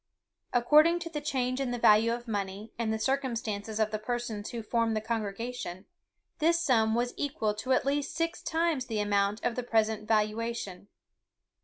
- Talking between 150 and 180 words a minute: Yes, average, 175 wpm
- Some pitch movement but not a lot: Yes, average, 3.5 semitones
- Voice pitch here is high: Yes, high, 230 Hz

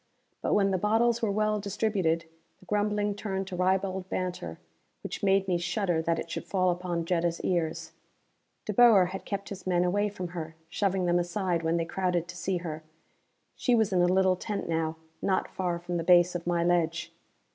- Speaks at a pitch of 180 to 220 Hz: Yes, medium, 185 Hz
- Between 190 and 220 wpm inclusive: Yes, average, 195 wpm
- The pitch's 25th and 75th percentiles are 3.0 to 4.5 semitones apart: No, narrow, 2.5 semitones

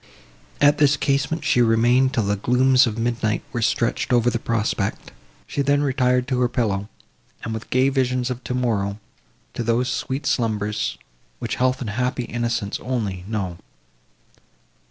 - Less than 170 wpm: Yes, average, 155 wpm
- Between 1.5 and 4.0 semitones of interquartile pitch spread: Yes, average, 2.7 semitones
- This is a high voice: No, low, 120 Hz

